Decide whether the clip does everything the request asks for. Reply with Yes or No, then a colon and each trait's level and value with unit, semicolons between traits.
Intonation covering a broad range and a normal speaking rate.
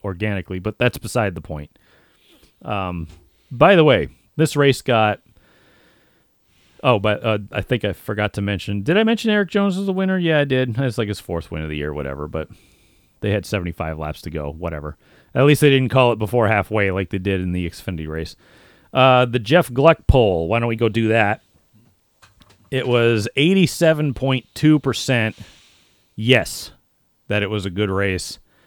Yes: wide, 5.7 semitones; average, 180 wpm